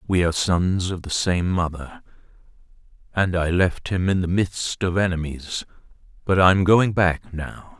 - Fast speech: No, average, 160 wpm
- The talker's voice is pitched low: Yes, very low, 90 Hz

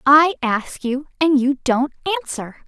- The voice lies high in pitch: Yes, very high, 280 Hz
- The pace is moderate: Yes, average, 155 wpm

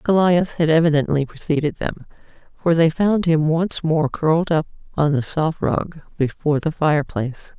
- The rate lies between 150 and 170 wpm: Yes, average, 160 wpm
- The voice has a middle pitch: Yes, medium, 155 Hz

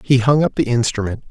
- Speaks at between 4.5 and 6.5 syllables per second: Yes, 6.0 syllables/s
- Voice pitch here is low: Yes, low, 125 Hz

